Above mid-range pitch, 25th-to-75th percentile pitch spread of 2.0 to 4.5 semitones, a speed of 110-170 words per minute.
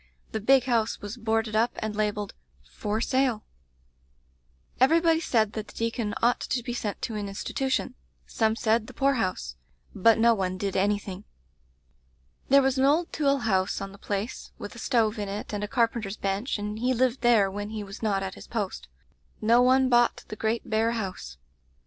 No: high, 220 Hz; average, 2.9 semitones; average, 185 wpm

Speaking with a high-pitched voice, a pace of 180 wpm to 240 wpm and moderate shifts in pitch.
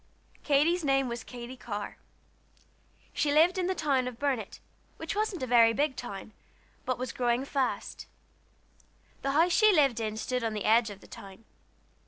Yes: very high, 255 Hz; average, 195 wpm; average, 4.5 semitones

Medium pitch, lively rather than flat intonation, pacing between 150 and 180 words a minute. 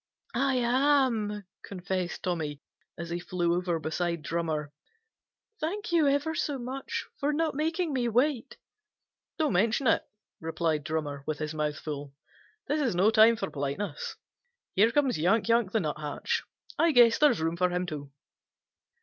No: high, 200 Hz; wide, 8.7 semitones; average, 155 wpm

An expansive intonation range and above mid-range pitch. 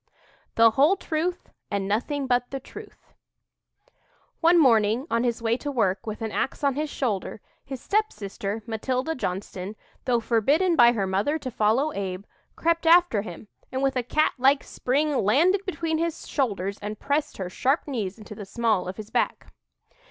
Yes: wide, 5.7 semitones; high, 245 Hz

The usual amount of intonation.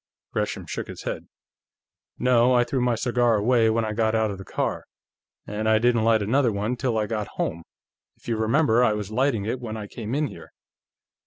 No: narrow, 2.2 semitones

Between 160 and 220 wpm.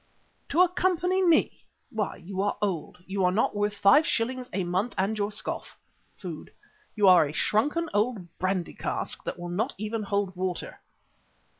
Yes: average, 165 wpm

